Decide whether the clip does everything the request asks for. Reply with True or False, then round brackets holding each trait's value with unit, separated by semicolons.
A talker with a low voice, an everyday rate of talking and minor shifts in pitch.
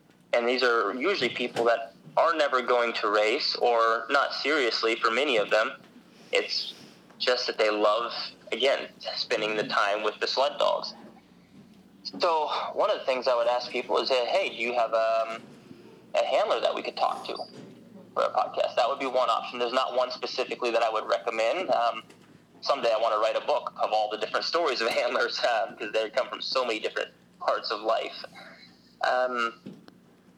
True (120 Hz; 190 wpm; 2.1 semitones)